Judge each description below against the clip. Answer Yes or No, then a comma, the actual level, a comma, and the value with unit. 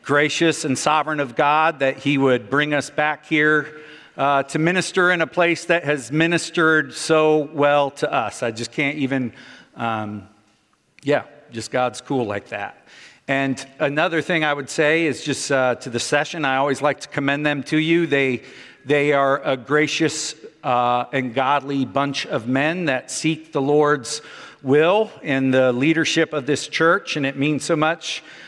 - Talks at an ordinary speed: Yes, average, 175 wpm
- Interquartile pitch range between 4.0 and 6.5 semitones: No, narrow, 2.5 semitones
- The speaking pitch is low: No, medium, 145 Hz